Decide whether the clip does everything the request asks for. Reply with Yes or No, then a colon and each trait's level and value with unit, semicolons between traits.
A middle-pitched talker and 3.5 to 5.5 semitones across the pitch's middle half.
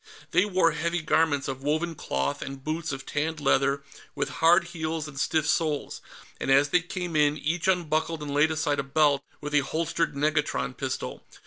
No: medium, 155 Hz; narrow, 2.5 semitones